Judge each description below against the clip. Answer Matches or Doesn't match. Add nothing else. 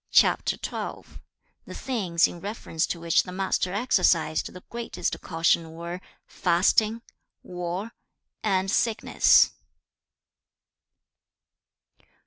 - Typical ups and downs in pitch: Matches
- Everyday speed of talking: Doesn't match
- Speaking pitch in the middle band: Matches